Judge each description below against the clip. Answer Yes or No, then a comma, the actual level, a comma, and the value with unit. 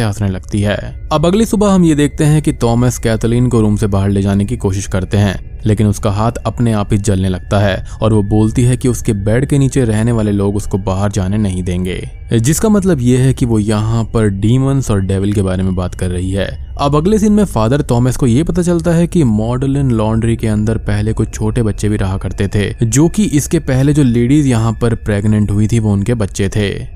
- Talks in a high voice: No, low, 110 Hz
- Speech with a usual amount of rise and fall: Yes, average, 4.1 semitones